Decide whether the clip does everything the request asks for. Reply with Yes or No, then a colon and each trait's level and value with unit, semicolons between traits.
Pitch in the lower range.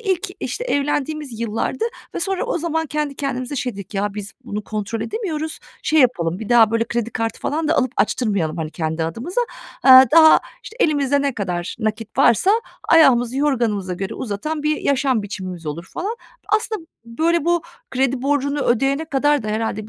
No: very high, 255 Hz